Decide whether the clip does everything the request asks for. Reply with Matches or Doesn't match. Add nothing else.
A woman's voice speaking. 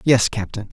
Doesn't match